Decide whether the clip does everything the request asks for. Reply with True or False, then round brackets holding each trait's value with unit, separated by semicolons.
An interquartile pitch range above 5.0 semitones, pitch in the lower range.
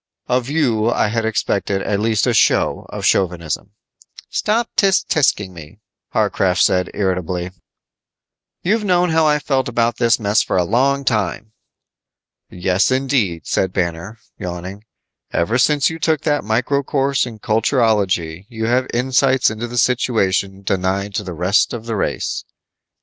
True (5.6 semitones; 110 Hz)